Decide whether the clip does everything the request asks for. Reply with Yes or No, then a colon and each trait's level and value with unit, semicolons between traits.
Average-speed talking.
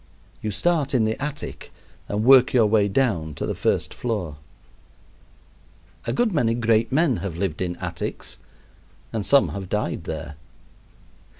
Yes: average, 145 wpm